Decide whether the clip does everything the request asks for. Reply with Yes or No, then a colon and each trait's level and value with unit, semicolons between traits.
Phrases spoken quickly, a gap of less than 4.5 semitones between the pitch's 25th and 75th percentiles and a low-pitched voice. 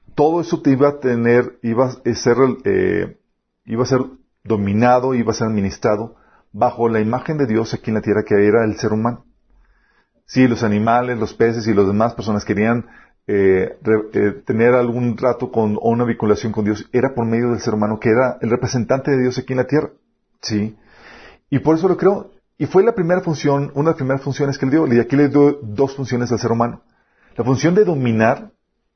Yes: fast, 215 wpm; average, 3.4 semitones; low, 120 Hz